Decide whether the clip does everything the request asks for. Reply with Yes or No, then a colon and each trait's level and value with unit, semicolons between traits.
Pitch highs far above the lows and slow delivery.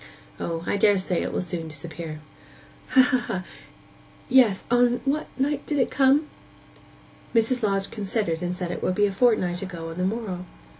No: wide, 5.7 semitones; average, 165 wpm